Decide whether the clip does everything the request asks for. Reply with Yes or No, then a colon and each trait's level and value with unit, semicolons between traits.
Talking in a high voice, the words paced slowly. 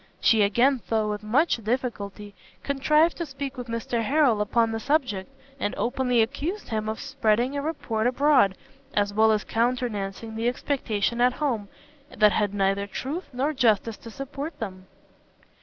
No: high, 235 Hz; average, 155 wpm